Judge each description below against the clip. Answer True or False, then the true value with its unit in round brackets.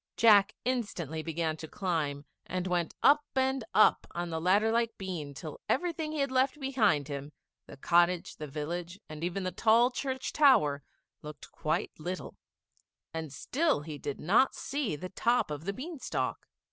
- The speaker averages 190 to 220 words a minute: False (170 wpm)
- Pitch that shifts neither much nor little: False (8.1 semitones)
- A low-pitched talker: False (185 Hz)